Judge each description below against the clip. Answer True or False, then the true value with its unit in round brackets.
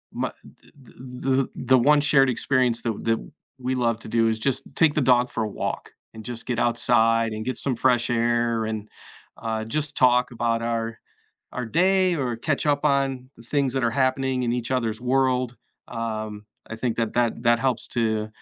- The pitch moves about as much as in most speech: False (2.3 semitones)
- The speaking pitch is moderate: False (120 Hz)